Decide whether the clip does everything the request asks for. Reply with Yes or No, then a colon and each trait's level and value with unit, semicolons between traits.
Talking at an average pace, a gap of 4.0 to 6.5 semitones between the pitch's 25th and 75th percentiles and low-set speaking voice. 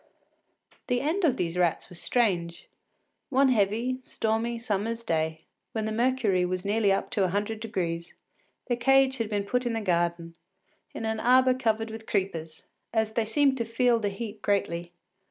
No: average, 175 wpm; average, 4.5 semitones; high, 220 Hz